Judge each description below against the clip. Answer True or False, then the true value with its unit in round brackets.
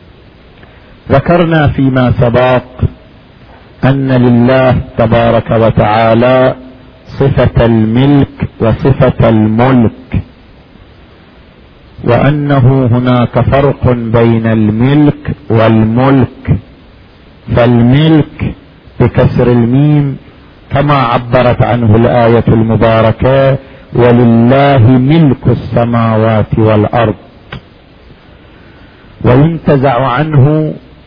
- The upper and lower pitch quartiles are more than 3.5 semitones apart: False (2.9 semitones)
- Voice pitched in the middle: False (120 Hz)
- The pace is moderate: False (60 wpm)